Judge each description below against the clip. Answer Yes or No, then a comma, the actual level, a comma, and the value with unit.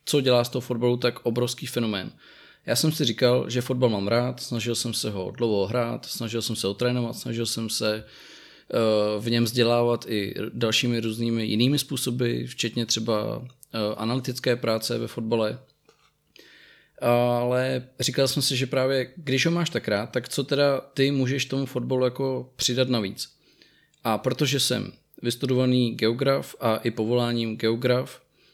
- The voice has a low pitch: Yes, low, 120 Hz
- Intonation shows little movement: Yes, narrow, 2.1 semitones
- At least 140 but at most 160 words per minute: Yes, average, 155 wpm